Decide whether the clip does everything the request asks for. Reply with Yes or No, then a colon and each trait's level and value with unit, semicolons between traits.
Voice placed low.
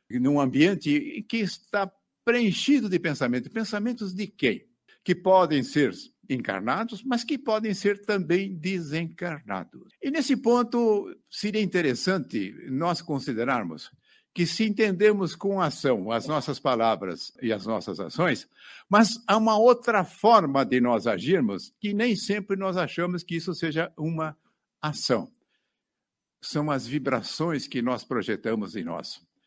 No: high, 190 Hz